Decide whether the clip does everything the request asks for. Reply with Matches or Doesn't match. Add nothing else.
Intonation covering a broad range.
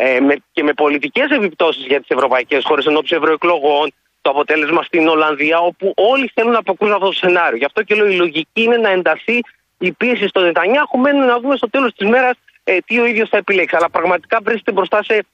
Matches